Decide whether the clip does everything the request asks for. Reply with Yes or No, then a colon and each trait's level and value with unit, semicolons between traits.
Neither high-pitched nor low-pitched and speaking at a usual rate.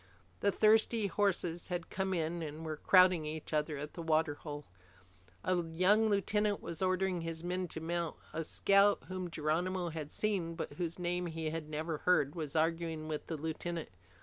Yes: medium, 170 Hz; average, 175 wpm